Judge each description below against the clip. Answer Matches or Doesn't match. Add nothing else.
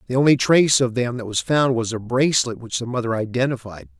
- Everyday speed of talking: Doesn't match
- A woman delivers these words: Doesn't match